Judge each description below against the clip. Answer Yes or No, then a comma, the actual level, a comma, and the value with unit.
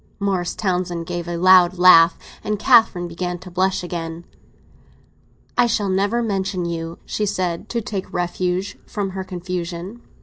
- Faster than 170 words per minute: No, average, 145 wpm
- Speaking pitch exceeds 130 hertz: Yes, medium, 185 Hz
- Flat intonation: Yes, narrow, 2.2 semitones